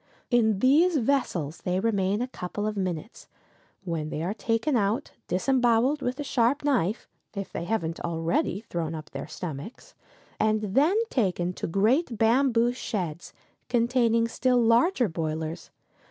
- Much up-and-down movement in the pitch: Yes, wide, 5.8 semitones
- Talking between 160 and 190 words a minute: No, average, 140 wpm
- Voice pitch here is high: Yes, high, 220 Hz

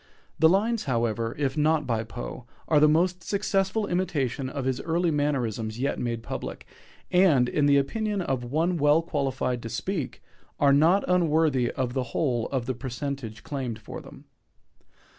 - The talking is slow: No, average, 160 wpm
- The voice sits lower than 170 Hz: Yes, medium, 140 Hz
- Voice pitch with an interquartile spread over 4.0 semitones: Yes, average, 5.1 semitones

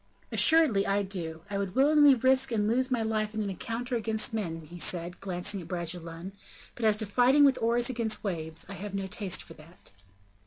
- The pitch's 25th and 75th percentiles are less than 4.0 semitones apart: No, average, 5.0 semitones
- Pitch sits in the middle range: No, high, 205 Hz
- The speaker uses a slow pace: No, average, 200 wpm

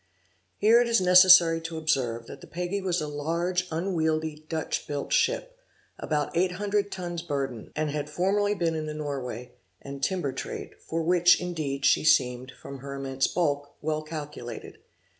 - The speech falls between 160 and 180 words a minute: Yes, average, 165 wpm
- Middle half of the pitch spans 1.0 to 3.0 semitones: No, average, 4.0 semitones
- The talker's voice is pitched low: No, medium, 160 Hz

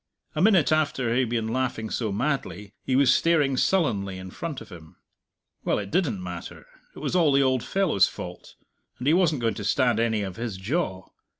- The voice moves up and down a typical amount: No, wide, 6.7 semitones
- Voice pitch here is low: Yes, low, 120 Hz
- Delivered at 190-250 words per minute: Yes, average, 200 wpm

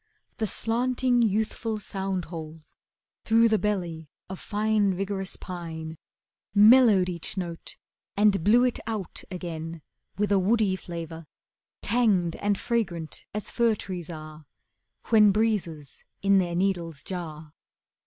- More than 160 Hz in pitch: Yes, high, 190 Hz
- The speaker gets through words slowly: Yes, slow, 125 wpm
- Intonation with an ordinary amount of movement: Yes, average, 4.3 semitones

